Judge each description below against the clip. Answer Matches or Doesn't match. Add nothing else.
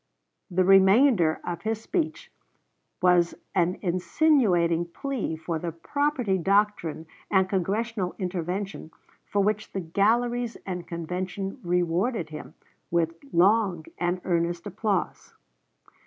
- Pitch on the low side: Doesn't match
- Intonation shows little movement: Doesn't match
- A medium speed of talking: Doesn't match